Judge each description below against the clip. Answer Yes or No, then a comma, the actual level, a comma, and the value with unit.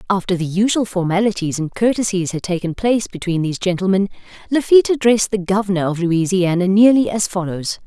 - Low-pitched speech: No, high, 195 Hz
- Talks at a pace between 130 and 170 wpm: Yes, average, 160 wpm